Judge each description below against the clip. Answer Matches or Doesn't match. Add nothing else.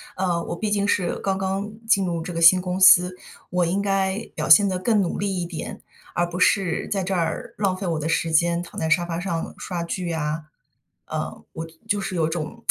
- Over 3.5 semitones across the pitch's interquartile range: Doesn't match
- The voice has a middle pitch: Matches